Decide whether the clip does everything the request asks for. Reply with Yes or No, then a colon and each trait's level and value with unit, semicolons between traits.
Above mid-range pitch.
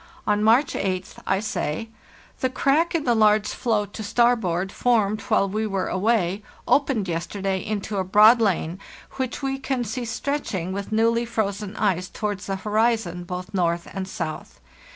Yes: high, 210 Hz